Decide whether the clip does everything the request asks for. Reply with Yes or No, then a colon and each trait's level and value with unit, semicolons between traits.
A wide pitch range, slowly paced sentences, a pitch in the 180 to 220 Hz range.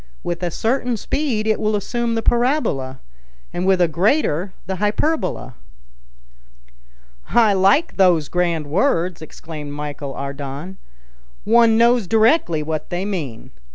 Yes: wide, 6.3 semitones; slow, 125 wpm; high, 190 Hz